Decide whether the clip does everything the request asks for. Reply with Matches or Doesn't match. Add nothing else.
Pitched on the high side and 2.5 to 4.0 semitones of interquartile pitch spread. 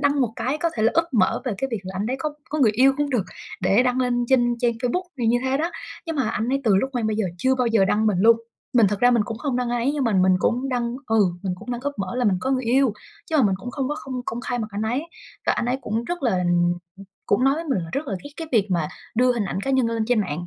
Matches